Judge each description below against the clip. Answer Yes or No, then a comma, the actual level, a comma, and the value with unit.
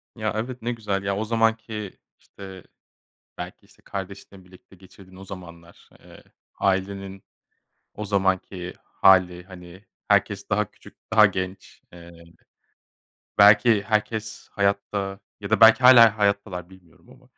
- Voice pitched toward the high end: No, low, 100 Hz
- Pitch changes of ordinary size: No, narrow, 2.3 semitones